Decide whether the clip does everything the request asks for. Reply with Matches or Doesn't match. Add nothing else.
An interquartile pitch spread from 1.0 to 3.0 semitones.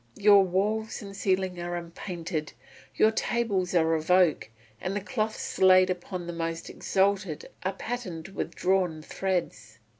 Matches